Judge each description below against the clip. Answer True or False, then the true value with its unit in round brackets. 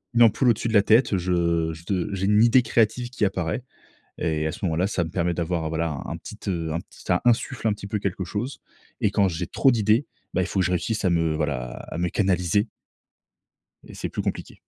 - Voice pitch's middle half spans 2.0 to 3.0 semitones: False (4.4 semitones)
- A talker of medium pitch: False (95 Hz)